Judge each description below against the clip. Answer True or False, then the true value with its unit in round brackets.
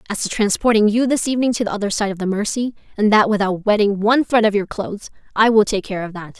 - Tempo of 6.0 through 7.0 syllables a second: True (6.6 syllables/s)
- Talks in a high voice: True (210 Hz)